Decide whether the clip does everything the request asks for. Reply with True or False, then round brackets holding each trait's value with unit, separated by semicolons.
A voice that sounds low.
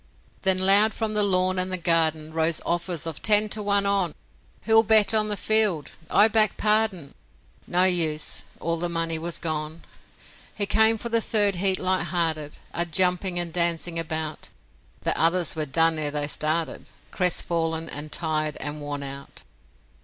False (175 Hz)